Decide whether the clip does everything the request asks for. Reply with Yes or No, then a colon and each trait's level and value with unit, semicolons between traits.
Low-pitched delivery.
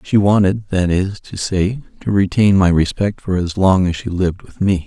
Yes: very low, 95 Hz